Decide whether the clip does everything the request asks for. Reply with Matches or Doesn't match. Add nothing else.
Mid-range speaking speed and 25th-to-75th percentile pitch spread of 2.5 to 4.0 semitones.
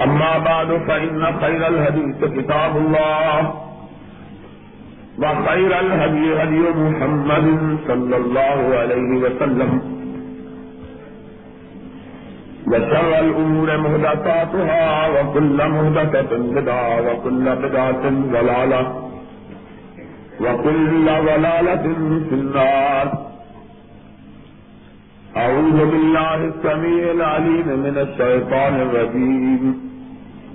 Doesn't match